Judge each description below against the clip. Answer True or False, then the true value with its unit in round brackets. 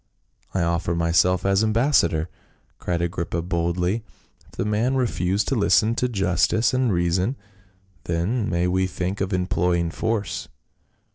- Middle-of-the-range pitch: False (90 Hz)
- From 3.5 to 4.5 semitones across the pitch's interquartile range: True (4.1 semitones)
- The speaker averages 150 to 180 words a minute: False (135 wpm)